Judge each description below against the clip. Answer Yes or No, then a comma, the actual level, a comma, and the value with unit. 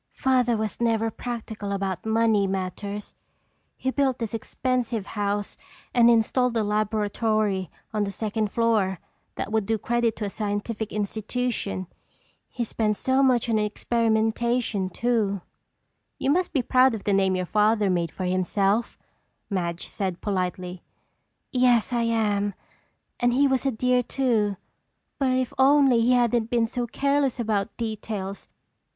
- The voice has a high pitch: Yes, high, 220 Hz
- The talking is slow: No, average, 145 wpm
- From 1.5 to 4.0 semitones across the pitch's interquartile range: Yes, average, 3.1 semitones